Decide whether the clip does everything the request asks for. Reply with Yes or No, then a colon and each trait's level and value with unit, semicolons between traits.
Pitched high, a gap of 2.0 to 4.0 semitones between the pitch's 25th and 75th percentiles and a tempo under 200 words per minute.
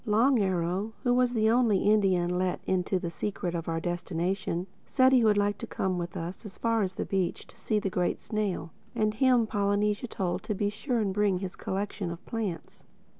No: high, 200 Hz; average, 3.1 semitones; fast, 205 wpm